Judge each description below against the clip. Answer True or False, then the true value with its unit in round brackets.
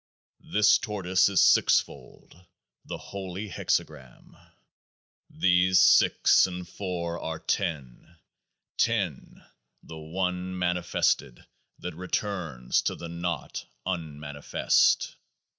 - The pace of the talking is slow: True (100 wpm)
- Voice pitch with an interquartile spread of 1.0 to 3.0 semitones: True (2.4 semitones)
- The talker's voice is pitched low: True (90 Hz)